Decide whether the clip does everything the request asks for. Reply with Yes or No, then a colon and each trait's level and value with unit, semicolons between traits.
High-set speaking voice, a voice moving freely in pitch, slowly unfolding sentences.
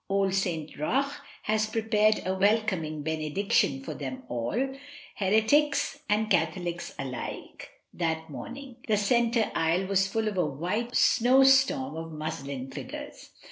Yes: high, 195 Hz; wide, 6.0 semitones; slow, 130 wpm